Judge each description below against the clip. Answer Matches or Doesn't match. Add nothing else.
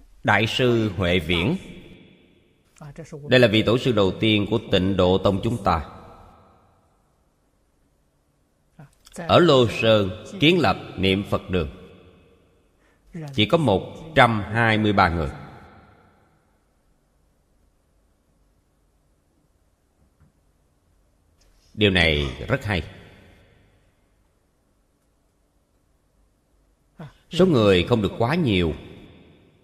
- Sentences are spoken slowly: Matches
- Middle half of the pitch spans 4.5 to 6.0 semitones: Matches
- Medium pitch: Doesn't match